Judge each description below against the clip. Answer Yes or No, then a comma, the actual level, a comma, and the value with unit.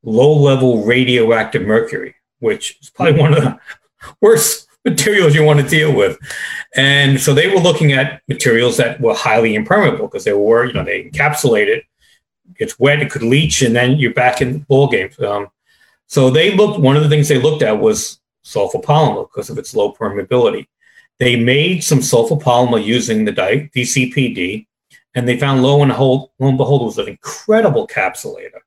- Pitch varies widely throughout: Yes, wide, 8.9 semitones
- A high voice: No, medium, 140 Hz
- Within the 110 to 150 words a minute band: No, average, 185 wpm